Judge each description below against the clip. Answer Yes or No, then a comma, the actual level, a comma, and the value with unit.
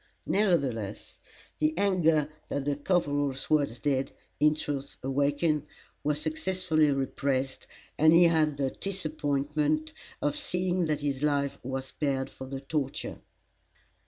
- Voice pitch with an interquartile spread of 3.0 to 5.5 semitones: No, narrow, 2.4 semitones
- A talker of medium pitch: Yes, medium, 145 Hz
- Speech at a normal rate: No, slow, 125 wpm